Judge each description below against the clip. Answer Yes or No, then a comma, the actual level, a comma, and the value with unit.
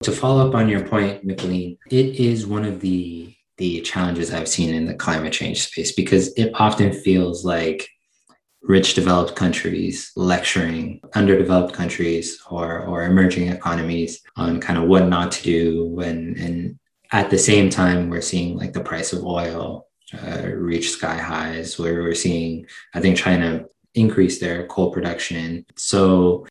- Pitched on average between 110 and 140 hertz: No, very low, 90 Hz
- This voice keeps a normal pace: Yes, average, 160 wpm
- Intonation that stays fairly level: Yes, narrow, 2.2 semitones